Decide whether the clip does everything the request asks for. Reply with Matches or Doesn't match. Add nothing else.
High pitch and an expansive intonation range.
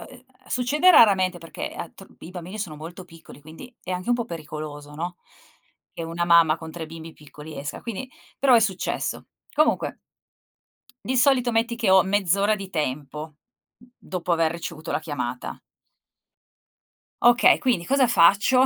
Doesn't match